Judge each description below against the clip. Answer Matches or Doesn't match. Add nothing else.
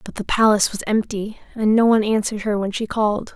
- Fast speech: Matches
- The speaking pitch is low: Doesn't match